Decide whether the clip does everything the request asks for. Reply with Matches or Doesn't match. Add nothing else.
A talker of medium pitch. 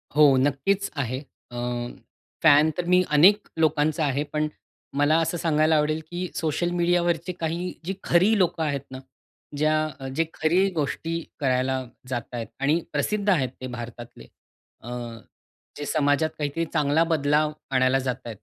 Matches